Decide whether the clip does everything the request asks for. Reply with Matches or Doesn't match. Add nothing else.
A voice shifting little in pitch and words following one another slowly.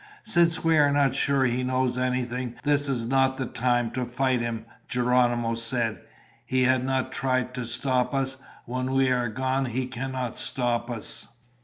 Doesn't match